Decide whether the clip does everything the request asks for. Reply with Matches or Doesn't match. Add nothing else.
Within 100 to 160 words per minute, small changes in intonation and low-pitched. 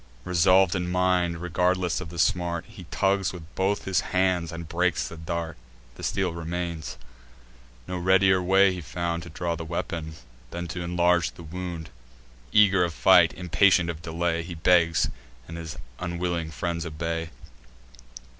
Matches